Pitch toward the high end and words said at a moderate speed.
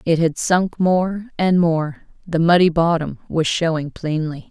No: medium, 165 Hz; average, 145 wpm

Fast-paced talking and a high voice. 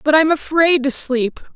No: average, 195 wpm; very high, 290 Hz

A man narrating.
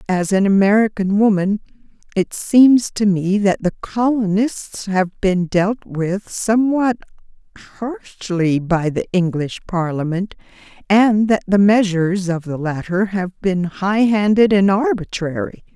No: female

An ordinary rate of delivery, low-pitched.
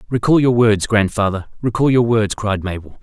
Yes: average, 160 wpm; low, 110 Hz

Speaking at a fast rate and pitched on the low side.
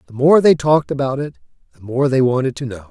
Yes: fast, 250 wpm; low, 130 Hz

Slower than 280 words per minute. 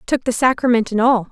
Yes: fast, 230 wpm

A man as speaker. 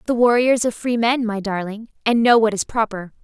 No: female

